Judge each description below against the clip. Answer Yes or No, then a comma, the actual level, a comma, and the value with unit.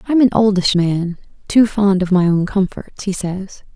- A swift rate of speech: Yes, fast, 210 wpm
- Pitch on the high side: Yes, high, 195 Hz